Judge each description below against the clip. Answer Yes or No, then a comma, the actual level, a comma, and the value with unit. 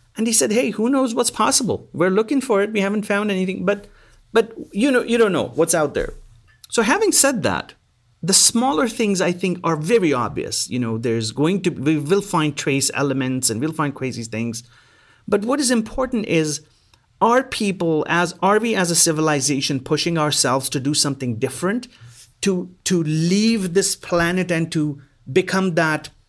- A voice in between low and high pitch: Yes, medium, 175 Hz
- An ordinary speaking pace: Yes, average, 185 wpm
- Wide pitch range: Yes, wide, 6.9 semitones